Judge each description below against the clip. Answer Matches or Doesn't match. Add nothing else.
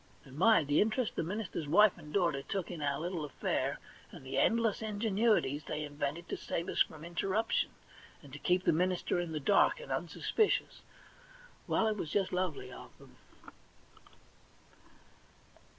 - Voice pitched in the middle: Matches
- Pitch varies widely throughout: Matches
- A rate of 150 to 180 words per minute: Matches